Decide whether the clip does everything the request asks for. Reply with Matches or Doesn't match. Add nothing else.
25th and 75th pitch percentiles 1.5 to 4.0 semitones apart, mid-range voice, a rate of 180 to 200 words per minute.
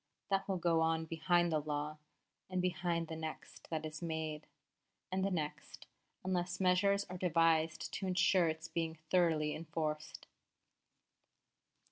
Doesn't match